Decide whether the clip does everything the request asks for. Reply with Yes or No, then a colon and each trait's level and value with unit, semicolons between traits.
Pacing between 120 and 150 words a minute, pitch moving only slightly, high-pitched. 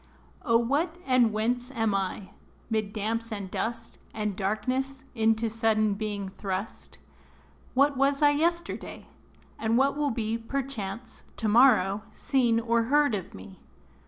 No: slow, 135 wpm; average, 3.8 semitones; high, 230 Hz